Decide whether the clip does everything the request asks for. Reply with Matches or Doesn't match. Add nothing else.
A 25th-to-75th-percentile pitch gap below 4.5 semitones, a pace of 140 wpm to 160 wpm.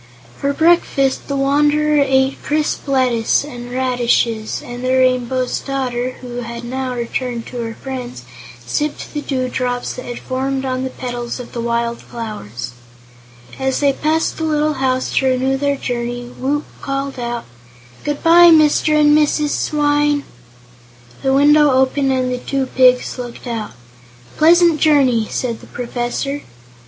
Matches